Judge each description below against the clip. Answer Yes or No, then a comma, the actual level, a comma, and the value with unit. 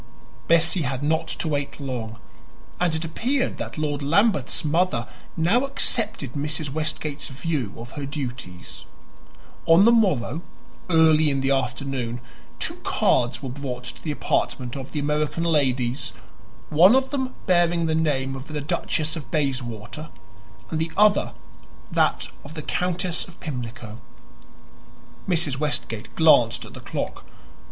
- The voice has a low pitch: No, medium, 150 Hz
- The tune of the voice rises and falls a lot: No, average, 3.9 semitones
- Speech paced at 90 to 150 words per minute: Yes, average, 140 wpm